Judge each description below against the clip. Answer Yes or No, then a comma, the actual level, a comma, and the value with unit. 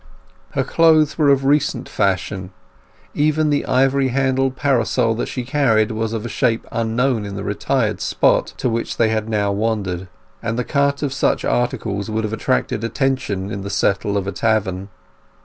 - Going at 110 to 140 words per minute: No, average, 175 wpm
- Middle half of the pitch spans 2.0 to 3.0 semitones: No, average, 4.6 semitones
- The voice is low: Yes, low, 115 Hz